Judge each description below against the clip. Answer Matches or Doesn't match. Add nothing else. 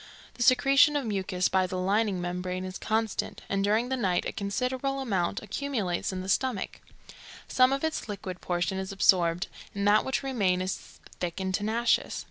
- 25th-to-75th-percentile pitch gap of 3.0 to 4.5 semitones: Doesn't match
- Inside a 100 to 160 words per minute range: Doesn't match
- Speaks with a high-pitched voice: Matches